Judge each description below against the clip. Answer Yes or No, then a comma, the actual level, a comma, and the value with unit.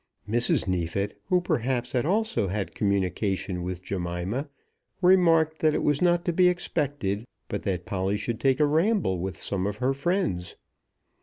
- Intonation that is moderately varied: No, wide, 8.8 semitones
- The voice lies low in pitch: Yes, low, 120 Hz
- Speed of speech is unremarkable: Yes, average, 160 wpm